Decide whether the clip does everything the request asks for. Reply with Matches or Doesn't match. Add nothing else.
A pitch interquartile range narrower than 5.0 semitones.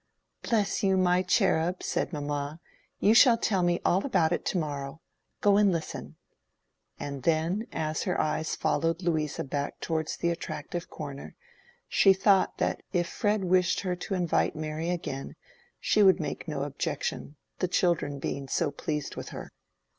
Matches